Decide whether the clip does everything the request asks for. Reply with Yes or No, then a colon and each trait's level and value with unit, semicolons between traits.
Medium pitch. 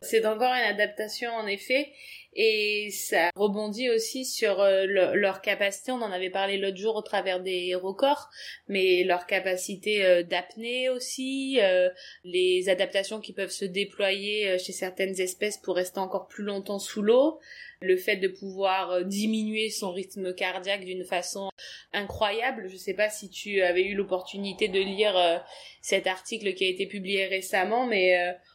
No: high, 195 Hz